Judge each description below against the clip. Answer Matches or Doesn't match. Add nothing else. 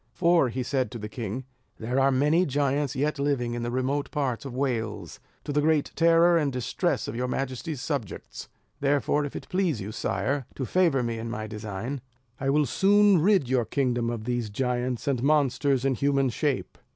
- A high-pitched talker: Doesn't match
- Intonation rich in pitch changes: Doesn't match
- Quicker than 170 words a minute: Matches